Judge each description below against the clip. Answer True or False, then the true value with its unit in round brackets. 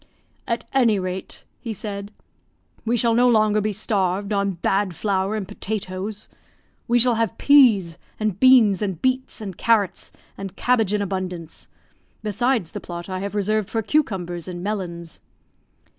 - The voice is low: False (205 Hz)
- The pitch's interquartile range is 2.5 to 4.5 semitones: True (3.2 semitones)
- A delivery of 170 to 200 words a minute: False (150 wpm)